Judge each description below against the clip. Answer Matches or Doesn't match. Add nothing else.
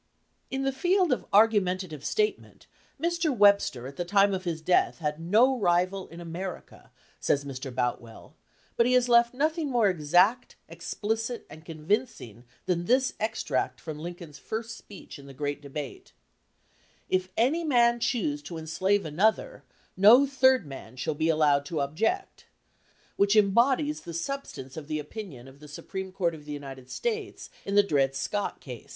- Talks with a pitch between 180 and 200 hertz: Matches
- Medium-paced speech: Matches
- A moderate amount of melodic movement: Doesn't match